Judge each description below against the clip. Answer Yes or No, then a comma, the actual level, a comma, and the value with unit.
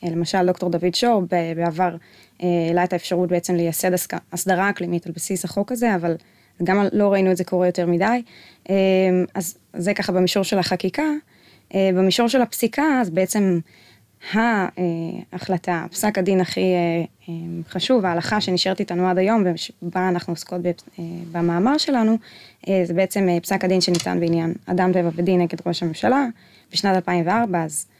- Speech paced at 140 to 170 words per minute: Yes, average, 165 wpm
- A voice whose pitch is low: No, medium, 185 Hz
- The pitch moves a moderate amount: No, narrow, 2.1 semitones